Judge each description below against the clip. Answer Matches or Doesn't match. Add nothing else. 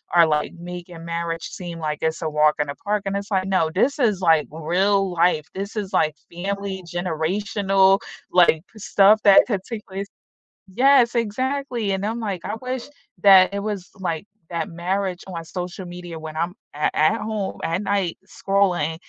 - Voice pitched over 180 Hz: Matches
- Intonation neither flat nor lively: Matches